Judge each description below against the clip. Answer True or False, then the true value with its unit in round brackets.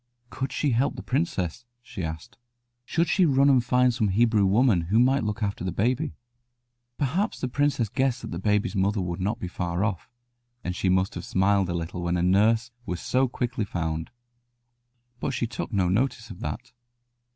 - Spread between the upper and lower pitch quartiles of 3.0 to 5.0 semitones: False (5.4 semitones)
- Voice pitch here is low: True (105 Hz)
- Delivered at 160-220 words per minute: True (190 wpm)